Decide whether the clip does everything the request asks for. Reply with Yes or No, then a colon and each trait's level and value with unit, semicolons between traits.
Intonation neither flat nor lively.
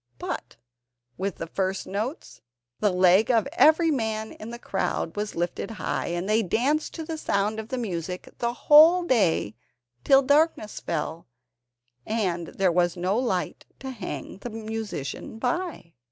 No: wide, 6.0 semitones